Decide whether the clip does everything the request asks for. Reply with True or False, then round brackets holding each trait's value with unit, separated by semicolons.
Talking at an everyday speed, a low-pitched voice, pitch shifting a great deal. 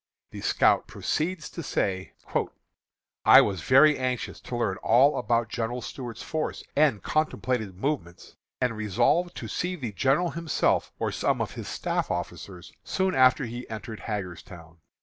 True (150 wpm; 120 Hz; 6.2 semitones)